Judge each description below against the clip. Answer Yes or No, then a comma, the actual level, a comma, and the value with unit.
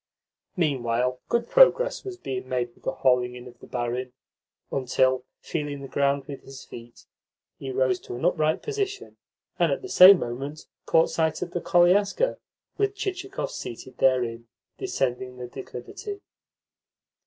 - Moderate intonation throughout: No, wide, 6.8 semitones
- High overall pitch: No, low, 135 Hz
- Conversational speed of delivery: Yes, average, 150 wpm